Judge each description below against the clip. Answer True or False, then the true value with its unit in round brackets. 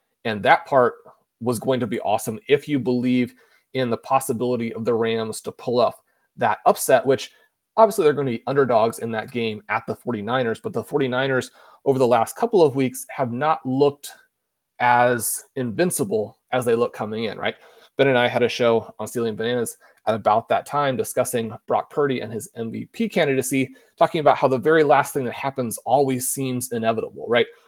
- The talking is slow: False (190 wpm)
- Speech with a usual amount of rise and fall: True (3.2 semitones)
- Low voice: True (130 Hz)